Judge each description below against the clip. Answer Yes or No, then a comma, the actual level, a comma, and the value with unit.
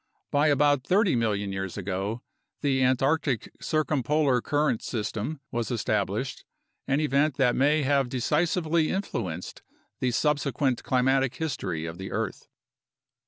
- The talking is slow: Yes, slow, 125 wpm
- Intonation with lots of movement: No, average, 4.7 semitones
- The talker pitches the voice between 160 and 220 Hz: No, low, 130 Hz